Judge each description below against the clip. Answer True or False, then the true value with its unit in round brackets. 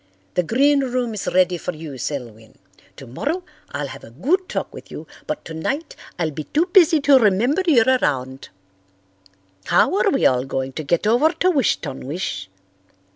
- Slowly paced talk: False (175 wpm)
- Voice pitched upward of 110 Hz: True (185 Hz)